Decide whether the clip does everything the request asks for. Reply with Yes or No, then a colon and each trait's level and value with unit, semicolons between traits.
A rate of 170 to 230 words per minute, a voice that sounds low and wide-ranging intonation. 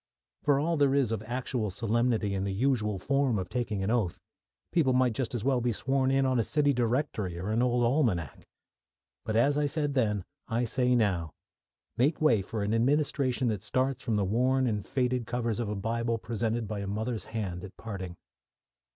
No: average, 195 wpm; low, 115 Hz; average, 3.8 semitones